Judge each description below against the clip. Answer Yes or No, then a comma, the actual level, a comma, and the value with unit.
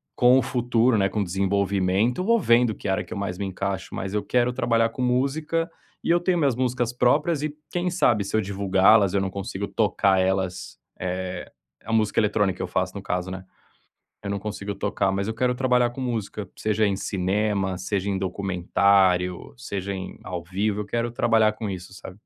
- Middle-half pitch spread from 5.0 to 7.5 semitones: No, average, 4.1 semitones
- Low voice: Yes, low, 100 Hz